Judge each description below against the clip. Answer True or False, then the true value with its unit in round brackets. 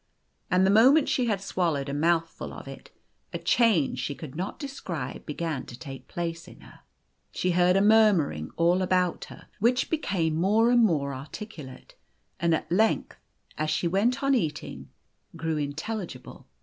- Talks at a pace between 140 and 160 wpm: False (175 wpm)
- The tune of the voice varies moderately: False (5.8 semitones)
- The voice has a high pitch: False (175 Hz)